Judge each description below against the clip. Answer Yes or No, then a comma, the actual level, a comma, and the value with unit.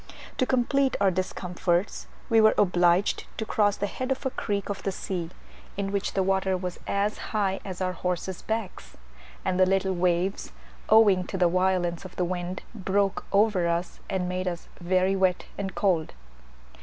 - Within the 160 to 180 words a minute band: Yes, average, 175 wpm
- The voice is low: No, high, 190 Hz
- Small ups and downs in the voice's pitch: Yes, narrow, 1.9 semitones